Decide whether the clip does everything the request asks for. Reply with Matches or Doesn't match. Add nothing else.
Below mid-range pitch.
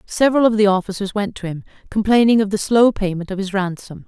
Doesn't match